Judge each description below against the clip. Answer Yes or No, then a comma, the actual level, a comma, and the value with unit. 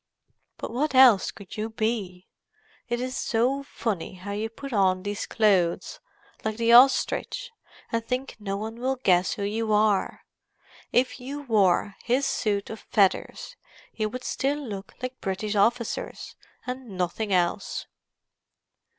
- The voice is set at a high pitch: Yes, high, 220 Hz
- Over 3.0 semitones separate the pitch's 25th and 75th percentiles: Yes, average, 4.0 semitones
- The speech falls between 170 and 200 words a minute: No, average, 140 wpm